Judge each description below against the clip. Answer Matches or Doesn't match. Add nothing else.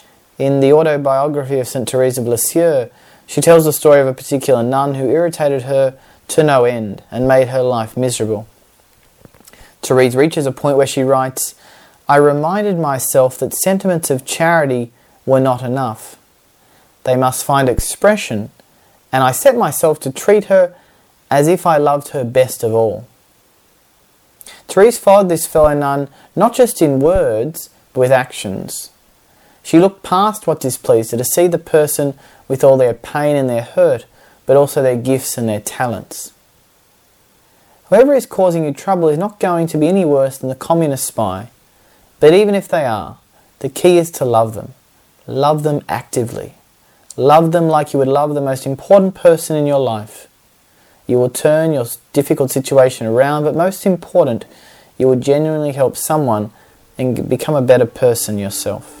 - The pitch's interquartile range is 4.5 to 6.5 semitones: Doesn't match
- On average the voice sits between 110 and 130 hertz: Doesn't match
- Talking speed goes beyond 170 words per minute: Doesn't match